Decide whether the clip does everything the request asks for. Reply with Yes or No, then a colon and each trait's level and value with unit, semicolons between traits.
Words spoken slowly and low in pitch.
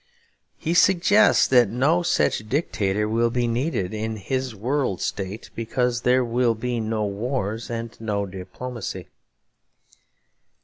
Yes: slow, 125 wpm; low, 115 Hz